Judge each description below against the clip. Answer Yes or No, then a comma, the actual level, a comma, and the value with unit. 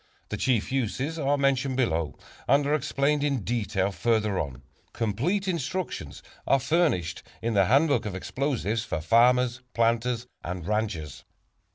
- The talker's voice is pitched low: Yes, low, 120 Hz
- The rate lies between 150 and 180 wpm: No, average, 140 wpm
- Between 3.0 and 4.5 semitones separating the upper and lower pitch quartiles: No, wide, 5.4 semitones